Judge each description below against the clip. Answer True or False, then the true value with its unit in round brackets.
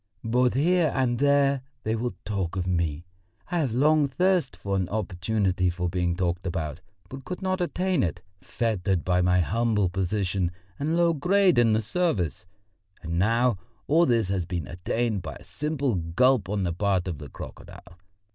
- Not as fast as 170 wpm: False (175 wpm)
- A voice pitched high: False (105 Hz)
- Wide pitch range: True (7.3 semitones)